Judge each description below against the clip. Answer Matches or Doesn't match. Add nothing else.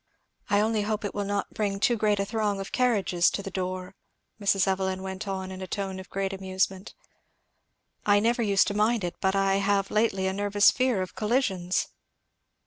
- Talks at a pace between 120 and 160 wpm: Doesn't match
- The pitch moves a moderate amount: Doesn't match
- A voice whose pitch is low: Doesn't match